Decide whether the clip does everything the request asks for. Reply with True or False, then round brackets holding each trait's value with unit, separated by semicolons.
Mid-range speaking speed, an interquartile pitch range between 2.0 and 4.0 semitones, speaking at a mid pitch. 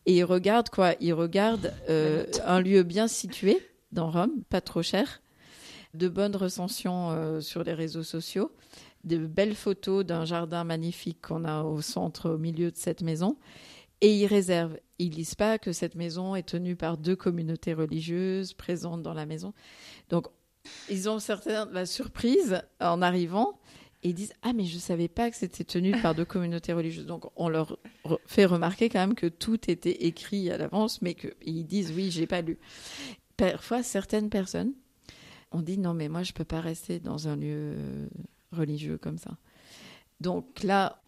True (180 wpm; 3.3 semitones; 175 Hz)